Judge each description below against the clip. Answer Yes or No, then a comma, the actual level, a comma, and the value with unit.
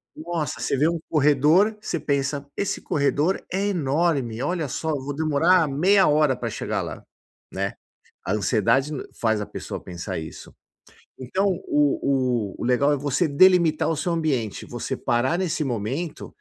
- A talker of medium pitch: Yes, medium, 145 Hz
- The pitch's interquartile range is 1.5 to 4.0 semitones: No, average, 4.4 semitones